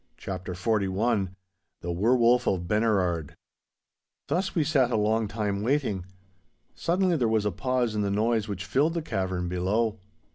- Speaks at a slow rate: No, average, 155 wpm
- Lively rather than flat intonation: No, average, 4.4 semitones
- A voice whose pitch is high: No, low, 110 Hz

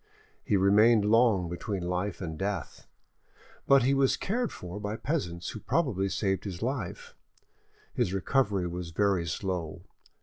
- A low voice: Yes, low, 100 Hz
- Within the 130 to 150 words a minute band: Yes, average, 140 wpm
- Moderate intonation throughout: Yes, average, 4.3 semitones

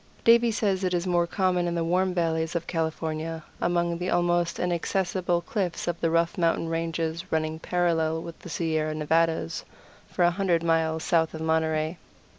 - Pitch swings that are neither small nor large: No, narrow, 1.6 semitones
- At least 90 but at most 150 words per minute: No, average, 170 wpm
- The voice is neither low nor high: Yes, medium, 170 Hz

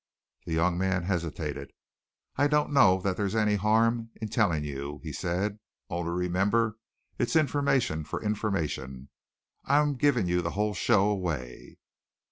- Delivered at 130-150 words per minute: Yes, average, 140 wpm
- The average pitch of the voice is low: Yes, very low, 95 Hz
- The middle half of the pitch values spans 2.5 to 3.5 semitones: No, average, 4.8 semitones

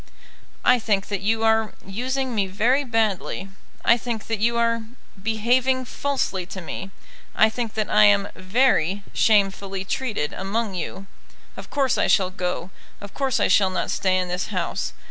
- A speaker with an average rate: Yes, average, 165 wpm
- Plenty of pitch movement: No, average, 3.4 semitones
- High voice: Yes, high, 215 Hz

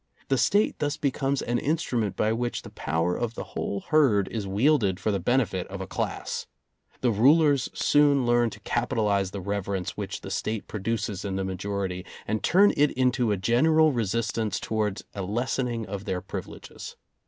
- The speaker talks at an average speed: Yes, average, 175 wpm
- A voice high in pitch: No, low, 110 Hz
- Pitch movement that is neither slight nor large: Yes, average, 4.7 semitones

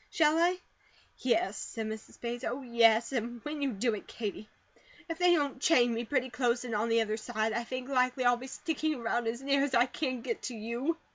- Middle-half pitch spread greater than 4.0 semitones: No, average, 3.2 semitones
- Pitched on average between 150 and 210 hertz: No, high, 245 Hz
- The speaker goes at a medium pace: No, fast, 220 wpm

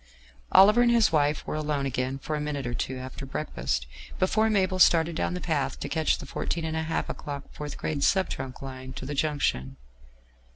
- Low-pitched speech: No, medium, 150 Hz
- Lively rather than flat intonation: No, average, 4.0 semitones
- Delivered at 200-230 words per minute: No, average, 190 wpm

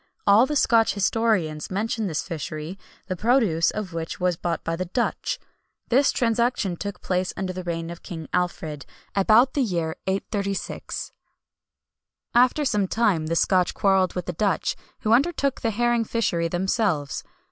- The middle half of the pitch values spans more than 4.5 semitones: Yes, average, 5.0 semitones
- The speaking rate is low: No, average, 155 wpm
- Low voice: No, high, 195 Hz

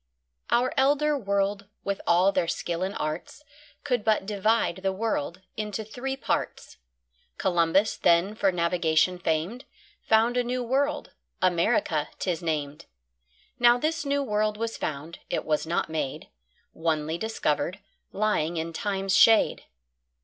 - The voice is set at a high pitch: Yes, high, 195 Hz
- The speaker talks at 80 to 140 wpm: Yes, slow, 135 wpm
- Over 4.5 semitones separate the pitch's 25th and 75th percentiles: Yes, average, 5.2 semitones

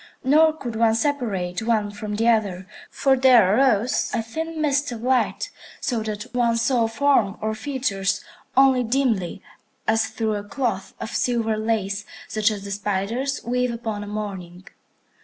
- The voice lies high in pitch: Yes, high, 225 Hz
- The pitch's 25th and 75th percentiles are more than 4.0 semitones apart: No, average, 3.6 semitones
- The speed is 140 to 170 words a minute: Yes, average, 160 wpm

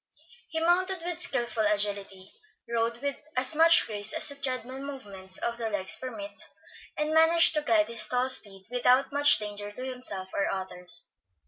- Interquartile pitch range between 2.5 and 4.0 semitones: No, wide, 5.6 semitones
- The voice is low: No, high, 245 Hz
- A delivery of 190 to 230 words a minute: No, average, 175 wpm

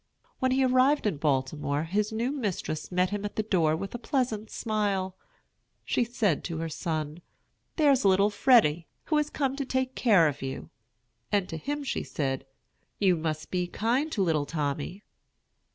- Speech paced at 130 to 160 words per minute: No, average, 170 wpm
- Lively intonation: Yes, wide, 7.5 semitones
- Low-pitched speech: No, high, 195 Hz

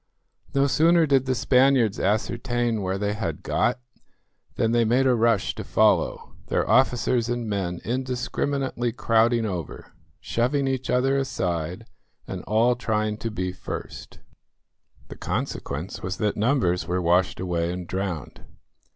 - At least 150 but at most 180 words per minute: No, average, 140 wpm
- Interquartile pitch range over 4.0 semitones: Yes, average, 5.2 semitones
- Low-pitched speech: Yes, low, 115 Hz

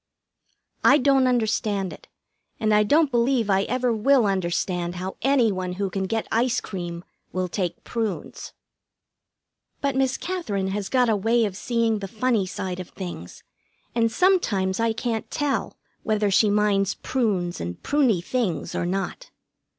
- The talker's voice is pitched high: Yes, high, 215 Hz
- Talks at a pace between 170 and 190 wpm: No, average, 155 wpm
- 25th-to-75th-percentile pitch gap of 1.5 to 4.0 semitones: No, average, 4.6 semitones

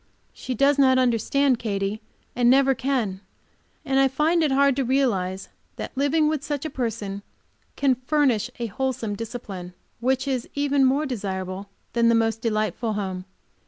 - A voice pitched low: No, very high, 250 Hz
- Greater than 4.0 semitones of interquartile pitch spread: Yes, average, 4.4 semitones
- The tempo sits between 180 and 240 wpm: No, average, 160 wpm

